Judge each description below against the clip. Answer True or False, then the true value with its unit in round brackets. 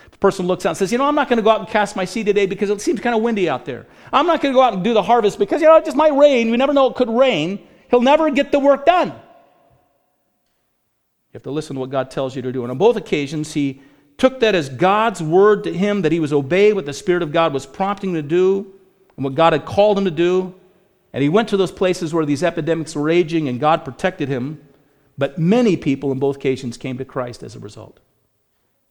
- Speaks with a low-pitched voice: False (185 Hz)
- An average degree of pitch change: False (7.3 semitones)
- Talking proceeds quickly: True (265 wpm)